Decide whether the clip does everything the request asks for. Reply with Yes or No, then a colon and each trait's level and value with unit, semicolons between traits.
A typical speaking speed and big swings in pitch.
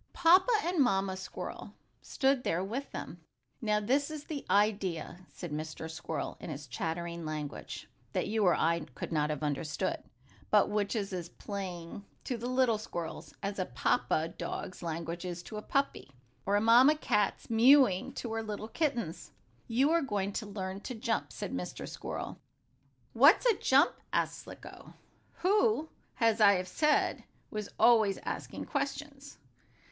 Yes: average, 160 wpm; wide, 7.2 semitones